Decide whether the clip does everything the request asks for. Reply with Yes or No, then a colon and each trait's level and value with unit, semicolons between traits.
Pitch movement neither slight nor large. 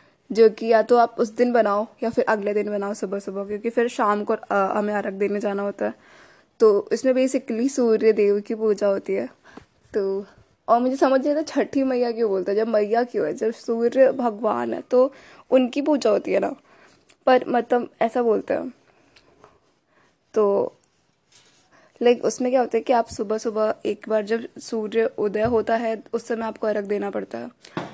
Yes: average, 3.0 semitones